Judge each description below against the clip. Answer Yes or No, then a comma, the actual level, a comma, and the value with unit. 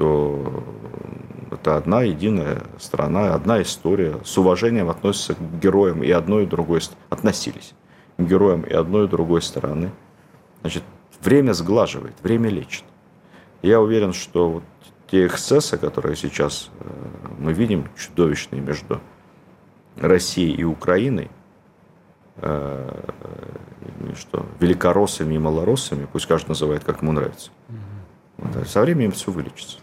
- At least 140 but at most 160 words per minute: No, average, 115 wpm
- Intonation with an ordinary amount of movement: Yes, average, 4.4 semitones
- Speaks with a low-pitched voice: Yes, very low, 90 Hz